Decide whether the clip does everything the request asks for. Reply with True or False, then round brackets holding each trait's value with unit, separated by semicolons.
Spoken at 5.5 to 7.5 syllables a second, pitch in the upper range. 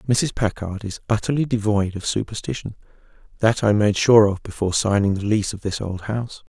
False (5.8 syllables/s; 105 Hz)